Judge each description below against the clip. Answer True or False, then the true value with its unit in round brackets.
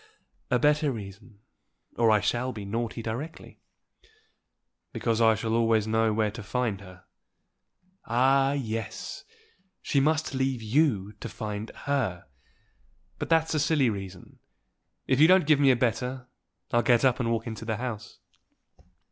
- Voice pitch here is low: True (115 Hz)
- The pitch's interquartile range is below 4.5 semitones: True (3.6 semitones)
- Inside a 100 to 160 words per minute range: True (150 wpm)